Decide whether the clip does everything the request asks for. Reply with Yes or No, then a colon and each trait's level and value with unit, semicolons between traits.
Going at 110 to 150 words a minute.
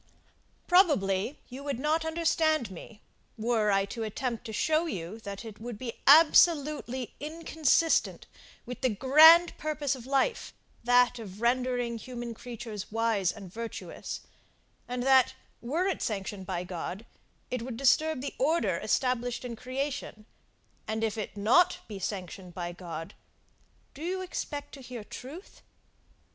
Yes: average, 140 wpm